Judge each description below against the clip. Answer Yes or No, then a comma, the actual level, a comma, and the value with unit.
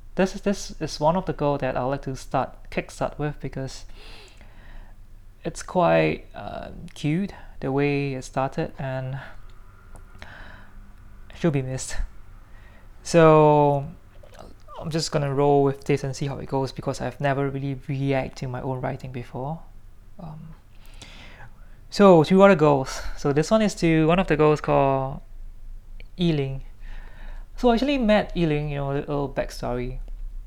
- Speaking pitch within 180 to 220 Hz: No, low, 135 Hz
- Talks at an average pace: Yes, average, 150 wpm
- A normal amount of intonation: No, wide, 6.6 semitones